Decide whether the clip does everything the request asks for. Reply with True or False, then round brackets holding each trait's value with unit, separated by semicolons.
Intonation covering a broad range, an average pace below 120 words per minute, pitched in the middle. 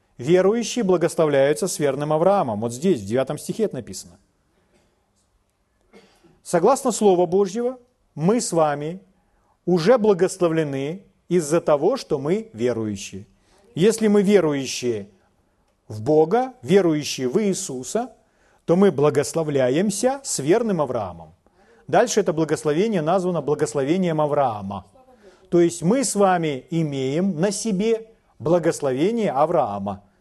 True (7.2 semitones; 110 wpm; 165 Hz)